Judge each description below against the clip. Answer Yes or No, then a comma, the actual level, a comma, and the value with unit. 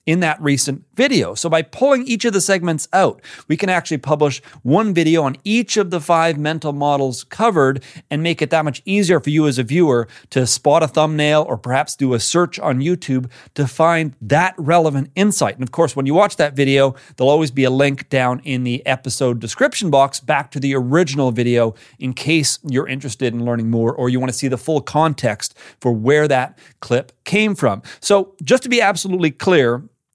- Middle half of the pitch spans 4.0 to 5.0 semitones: Yes, average, 4.4 semitones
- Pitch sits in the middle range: Yes, medium, 145 Hz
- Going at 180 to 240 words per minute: Yes, fast, 205 wpm